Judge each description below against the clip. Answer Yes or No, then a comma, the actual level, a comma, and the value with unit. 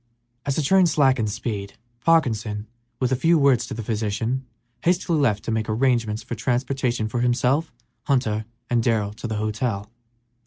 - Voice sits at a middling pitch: No, low, 120 Hz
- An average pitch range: Yes, average, 3.8 semitones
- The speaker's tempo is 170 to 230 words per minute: No, average, 160 wpm